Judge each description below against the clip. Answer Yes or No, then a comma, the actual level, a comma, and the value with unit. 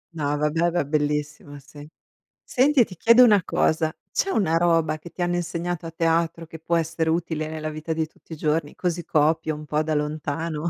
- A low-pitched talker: No, medium, 160 Hz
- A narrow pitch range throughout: Yes, narrow, 2.0 semitones